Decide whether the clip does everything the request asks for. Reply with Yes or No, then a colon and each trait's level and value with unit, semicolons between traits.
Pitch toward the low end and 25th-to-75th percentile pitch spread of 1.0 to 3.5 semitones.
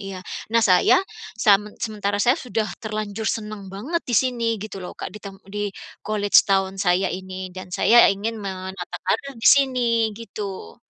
No: high, 205 Hz; average, 2.9 semitones